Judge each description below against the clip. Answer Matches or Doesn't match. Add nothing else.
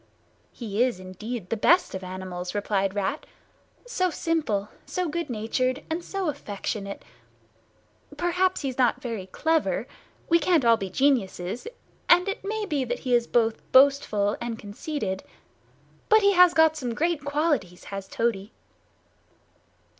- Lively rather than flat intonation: Matches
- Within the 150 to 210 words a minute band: Doesn't match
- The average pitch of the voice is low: Doesn't match